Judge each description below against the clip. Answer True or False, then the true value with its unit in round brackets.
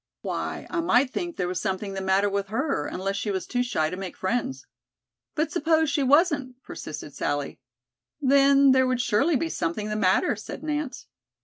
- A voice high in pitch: True (245 Hz)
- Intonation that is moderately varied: False (6.7 semitones)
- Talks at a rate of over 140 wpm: True (185 wpm)